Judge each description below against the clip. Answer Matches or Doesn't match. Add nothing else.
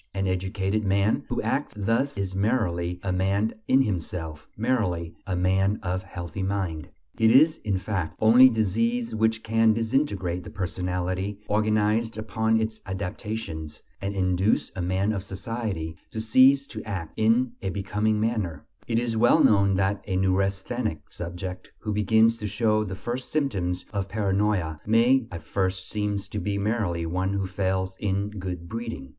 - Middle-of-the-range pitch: Doesn't match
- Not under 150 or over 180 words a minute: Matches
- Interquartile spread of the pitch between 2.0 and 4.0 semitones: Matches